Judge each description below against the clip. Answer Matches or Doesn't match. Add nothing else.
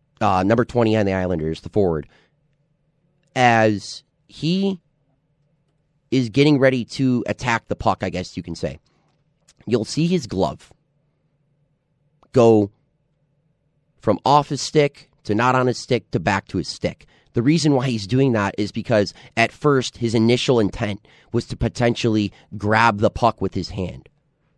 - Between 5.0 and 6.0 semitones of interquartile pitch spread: Matches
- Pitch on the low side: Matches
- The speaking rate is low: Doesn't match